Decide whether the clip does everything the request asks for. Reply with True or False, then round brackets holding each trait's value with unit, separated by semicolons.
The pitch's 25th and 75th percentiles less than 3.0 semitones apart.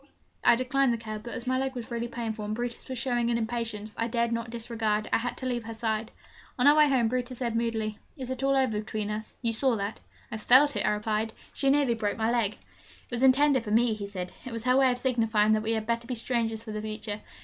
True (2.5 semitones)